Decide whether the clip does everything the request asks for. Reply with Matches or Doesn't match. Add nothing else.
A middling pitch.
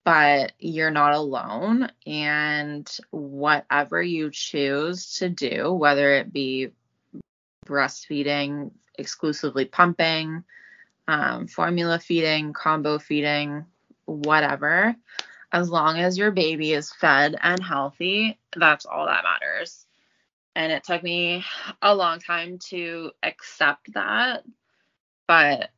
Matches